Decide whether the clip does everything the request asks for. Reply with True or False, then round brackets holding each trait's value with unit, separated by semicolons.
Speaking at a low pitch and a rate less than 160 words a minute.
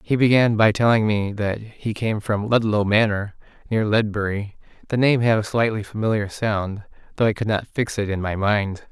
False (105 Hz; 195 wpm)